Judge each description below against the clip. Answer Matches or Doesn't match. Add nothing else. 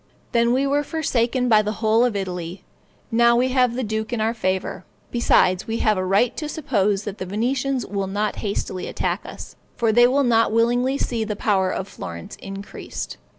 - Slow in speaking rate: Doesn't match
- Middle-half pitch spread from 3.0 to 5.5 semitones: Matches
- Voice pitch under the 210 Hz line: Doesn't match